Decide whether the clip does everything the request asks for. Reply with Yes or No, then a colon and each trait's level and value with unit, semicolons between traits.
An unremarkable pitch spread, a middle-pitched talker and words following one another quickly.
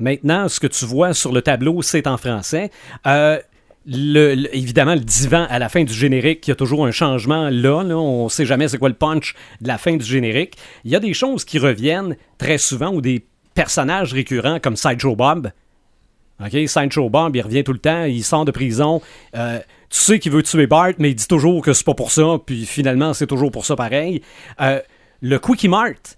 Yes: average, 3.4 semitones; medium, 145 Hz; fast, 225 wpm